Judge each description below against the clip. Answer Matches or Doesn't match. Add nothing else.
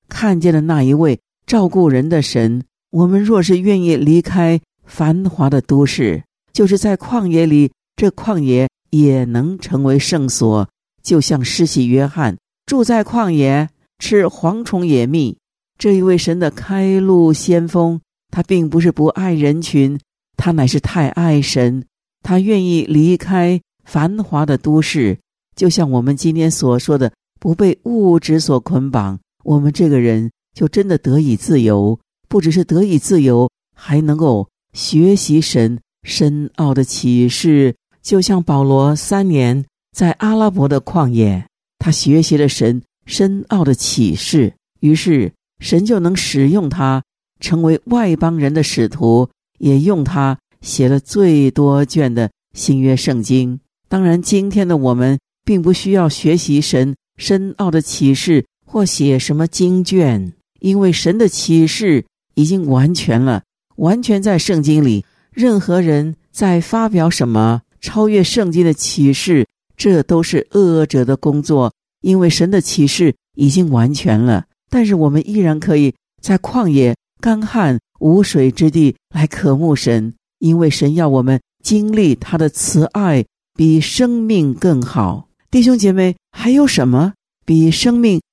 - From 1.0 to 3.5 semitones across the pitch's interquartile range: Doesn't match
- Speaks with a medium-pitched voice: Matches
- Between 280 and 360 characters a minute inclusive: Doesn't match